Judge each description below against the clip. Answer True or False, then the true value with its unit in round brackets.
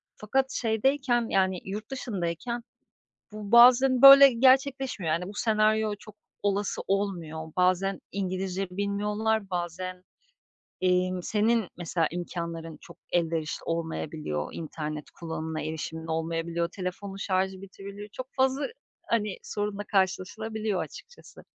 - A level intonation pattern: False (4.3 semitones)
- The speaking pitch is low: False (195 Hz)